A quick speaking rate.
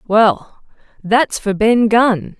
No: slow, 125 wpm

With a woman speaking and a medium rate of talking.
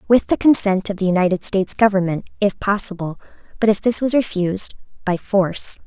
Yes: female; average, 175 wpm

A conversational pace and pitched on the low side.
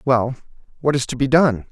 No: fast, 210 wpm; low, 130 Hz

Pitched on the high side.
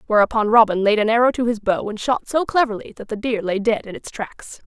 Yes: high, 220 Hz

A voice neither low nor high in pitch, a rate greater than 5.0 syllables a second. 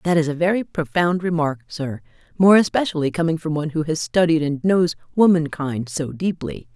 Yes: medium, 160 Hz; 5.5 syllables/s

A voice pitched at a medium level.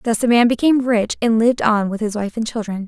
No: high, 225 Hz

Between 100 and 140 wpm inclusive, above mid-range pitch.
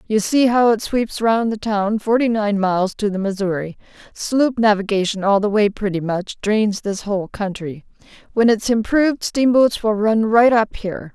No: average, 180 wpm; high, 215 Hz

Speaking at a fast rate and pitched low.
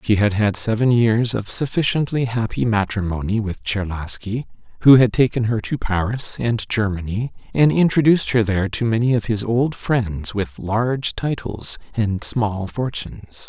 No: average, 155 wpm; low, 110 Hz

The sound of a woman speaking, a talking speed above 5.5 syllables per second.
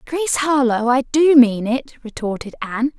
No: female; 5.3 syllables/s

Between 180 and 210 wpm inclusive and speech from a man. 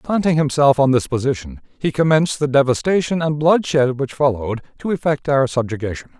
No: average, 165 wpm; male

